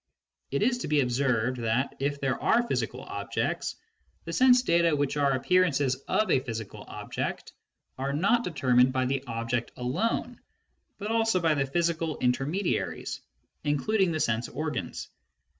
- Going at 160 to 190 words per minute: No, average, 150 wpm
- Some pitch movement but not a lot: No, wide, 5.9 semitones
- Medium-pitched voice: Yes, medium, 145 Hz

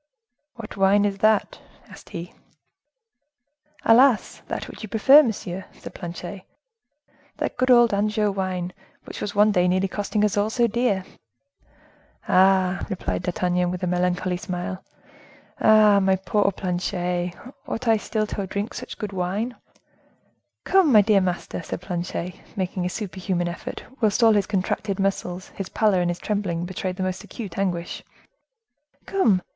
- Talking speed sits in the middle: Yes, average, 150 wpm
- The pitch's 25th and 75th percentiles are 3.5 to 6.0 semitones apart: No, average, 2.8 semitones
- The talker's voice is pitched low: No, high, 195 Hz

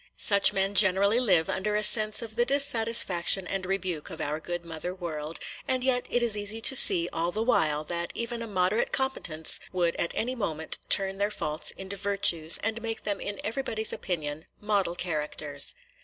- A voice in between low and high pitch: No, high, 195 Hz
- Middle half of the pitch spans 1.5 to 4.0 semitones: No, average, 4.5 semitones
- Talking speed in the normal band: Yes, average, 185 wpm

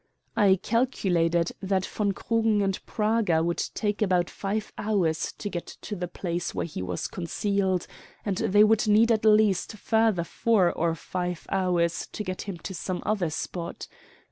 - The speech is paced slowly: No, average, 165 wpm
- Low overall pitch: No, high, 190 Hz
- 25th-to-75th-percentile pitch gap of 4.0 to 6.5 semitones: No, average, 3.4 semitones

